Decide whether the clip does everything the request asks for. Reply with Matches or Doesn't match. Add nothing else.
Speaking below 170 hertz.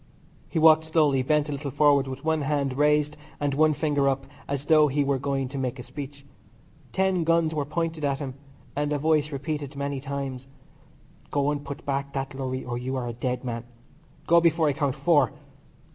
Matches